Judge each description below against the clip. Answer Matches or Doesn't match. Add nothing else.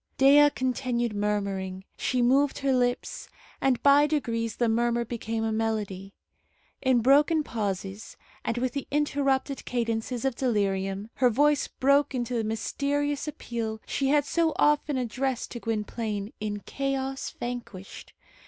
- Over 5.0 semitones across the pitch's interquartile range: Doesn't match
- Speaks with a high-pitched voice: Matches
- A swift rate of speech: Doesn't match